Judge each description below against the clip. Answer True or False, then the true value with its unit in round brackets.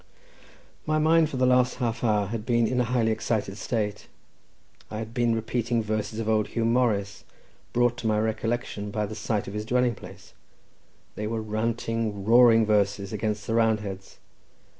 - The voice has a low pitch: True (110 Hz)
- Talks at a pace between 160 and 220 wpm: True (170 wpm)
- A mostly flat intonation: True (2.0 semitones)